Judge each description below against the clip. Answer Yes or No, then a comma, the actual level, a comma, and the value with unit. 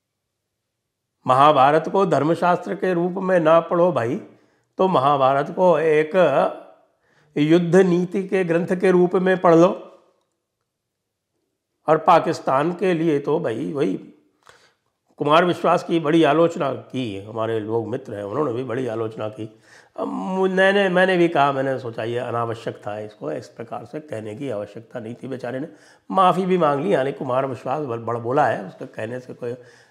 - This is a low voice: No, medium, 145 Hz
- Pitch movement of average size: No, wide, 7.2 semitones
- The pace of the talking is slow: No, average, 155 wpm